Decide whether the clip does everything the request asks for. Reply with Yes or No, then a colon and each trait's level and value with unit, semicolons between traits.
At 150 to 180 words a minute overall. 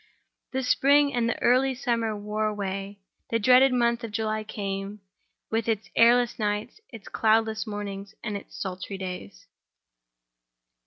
No: average, 140 wpm